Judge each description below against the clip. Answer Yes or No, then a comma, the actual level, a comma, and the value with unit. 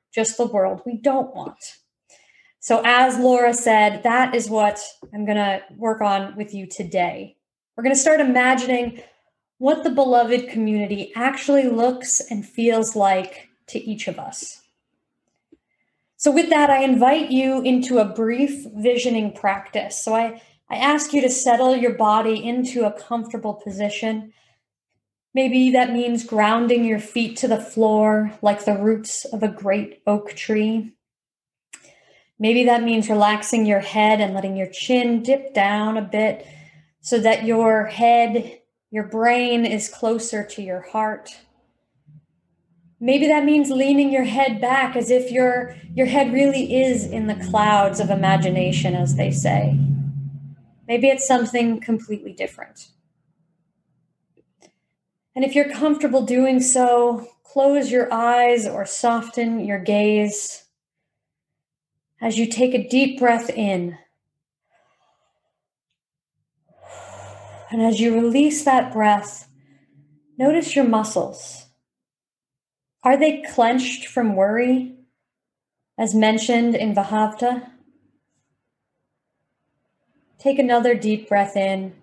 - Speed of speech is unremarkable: No, slow, 130 wpm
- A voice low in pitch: No, high, 225 Hz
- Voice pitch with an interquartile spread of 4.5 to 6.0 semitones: No, average, 3.4 semitones